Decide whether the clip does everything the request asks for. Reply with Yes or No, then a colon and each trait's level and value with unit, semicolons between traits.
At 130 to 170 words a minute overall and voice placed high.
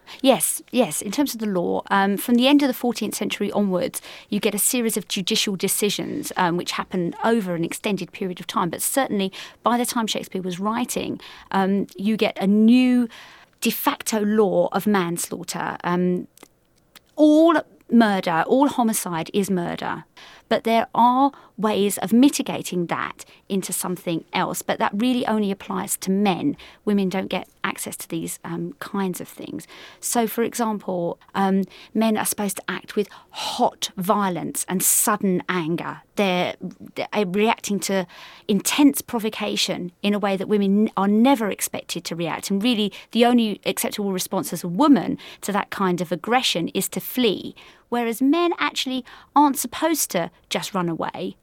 Yes: average, 165 wpm; high, 205 Hz